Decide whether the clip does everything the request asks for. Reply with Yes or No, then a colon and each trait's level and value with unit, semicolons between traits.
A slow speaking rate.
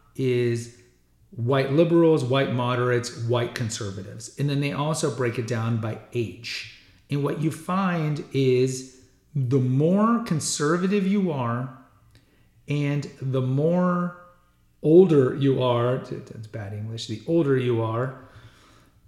Yes: slow, 125 wpm